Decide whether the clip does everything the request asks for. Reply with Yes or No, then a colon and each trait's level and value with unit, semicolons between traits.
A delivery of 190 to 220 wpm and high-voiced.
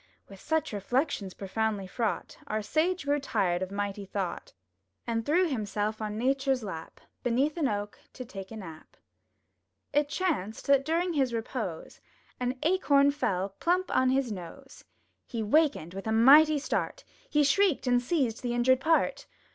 No: average, 160 wpm; high, 245 Hz